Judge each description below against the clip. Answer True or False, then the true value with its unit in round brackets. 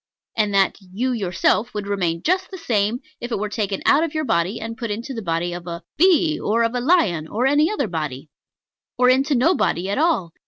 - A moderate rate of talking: False (225 wpm)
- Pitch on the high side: True (225 Hz)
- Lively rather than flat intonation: True (6.6 semitones)